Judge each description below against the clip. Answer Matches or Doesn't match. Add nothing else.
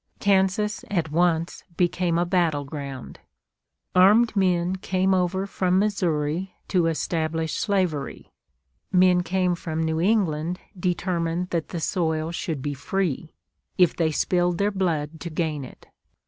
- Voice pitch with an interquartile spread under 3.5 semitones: Matches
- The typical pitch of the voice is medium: Matches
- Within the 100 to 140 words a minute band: Matches